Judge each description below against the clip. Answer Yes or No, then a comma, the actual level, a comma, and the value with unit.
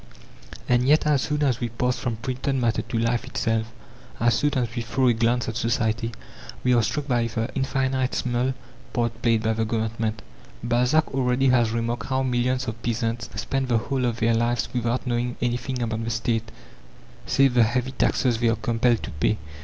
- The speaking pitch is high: No, low, 120 Hz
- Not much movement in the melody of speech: Yes, narrow, 2.0 semitones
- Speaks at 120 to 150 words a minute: No, average, 190 wpm